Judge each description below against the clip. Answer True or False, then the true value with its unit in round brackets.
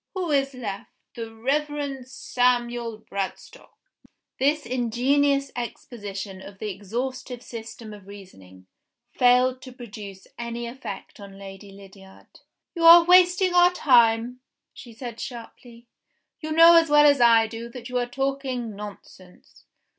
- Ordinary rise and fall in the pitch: True (4.5 semitones)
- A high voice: True (240 Hz)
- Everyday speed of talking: False (130 wpm)